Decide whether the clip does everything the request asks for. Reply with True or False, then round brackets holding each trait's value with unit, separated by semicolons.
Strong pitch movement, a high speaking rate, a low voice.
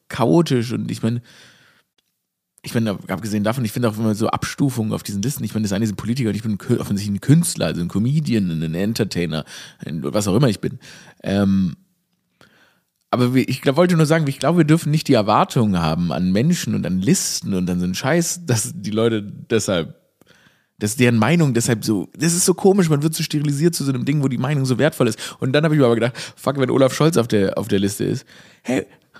True (6.7 semitones; 235 wpm; 125 Hz)